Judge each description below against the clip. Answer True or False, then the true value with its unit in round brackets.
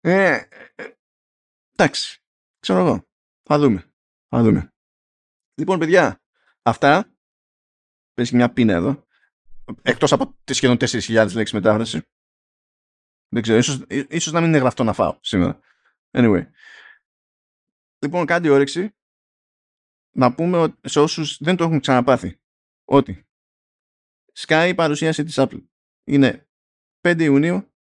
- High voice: False (135 Hz)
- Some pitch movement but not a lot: False (6.3 semitones)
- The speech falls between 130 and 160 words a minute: False (120 wpm)